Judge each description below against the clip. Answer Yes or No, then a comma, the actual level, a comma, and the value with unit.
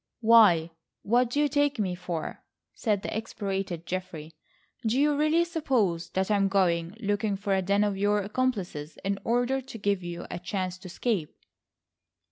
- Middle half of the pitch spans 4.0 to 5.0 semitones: Yes, average, 4.3 semitones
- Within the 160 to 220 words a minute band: Yes, average, 170 wpm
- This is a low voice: No, high, 200 Hz